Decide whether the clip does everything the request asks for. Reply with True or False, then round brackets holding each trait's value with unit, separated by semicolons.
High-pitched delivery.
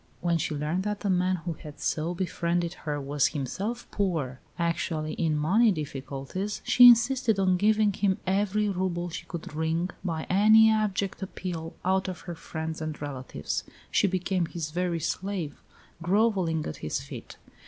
False (175 Hz)